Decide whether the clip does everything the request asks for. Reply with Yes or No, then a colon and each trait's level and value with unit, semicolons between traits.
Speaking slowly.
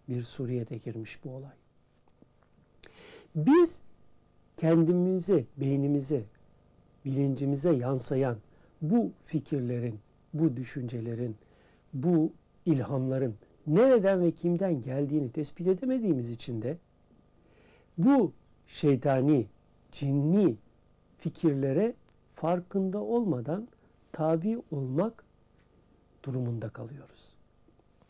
Yes: slow, 75 wpm